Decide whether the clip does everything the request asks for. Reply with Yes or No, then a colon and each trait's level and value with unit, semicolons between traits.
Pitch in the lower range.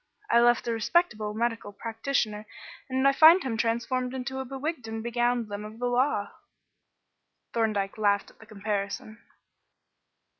No: high, 230 Hz